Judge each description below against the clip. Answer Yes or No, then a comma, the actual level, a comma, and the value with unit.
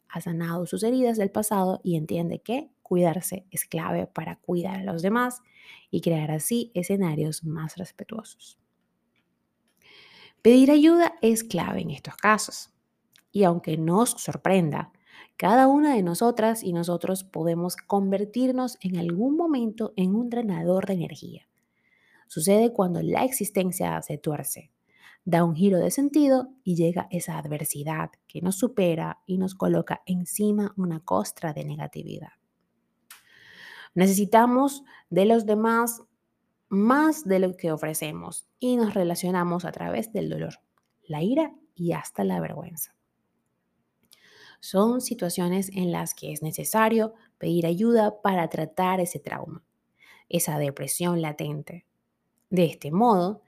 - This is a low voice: No, medium, 185 Hz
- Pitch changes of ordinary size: Yes, average, 4.8 semitones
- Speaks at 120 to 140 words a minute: Yes, average, 130 wpm